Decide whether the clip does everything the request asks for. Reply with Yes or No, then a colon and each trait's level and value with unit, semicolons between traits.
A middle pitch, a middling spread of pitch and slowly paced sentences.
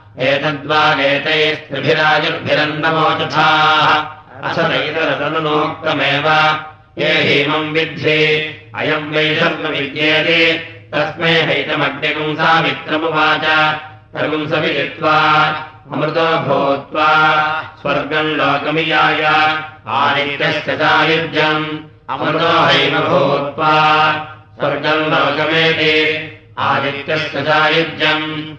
No: medium, 155 Hz; narrow, 0.6 semitones; slow, 50 wpm